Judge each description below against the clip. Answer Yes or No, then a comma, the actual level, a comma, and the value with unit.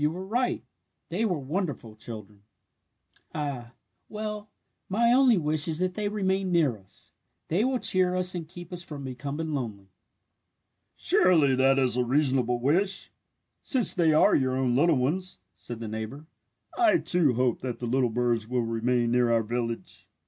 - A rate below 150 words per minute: No, average, 170 wpm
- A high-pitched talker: No, medium, 145 Hz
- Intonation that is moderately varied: No, wide, 7.0 semitones